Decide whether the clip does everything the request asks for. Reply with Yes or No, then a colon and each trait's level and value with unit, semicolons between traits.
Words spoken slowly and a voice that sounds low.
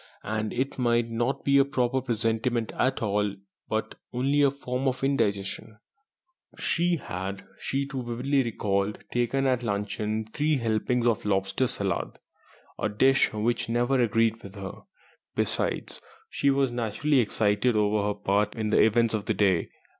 No: average, 155 wpm; low, 115 Hz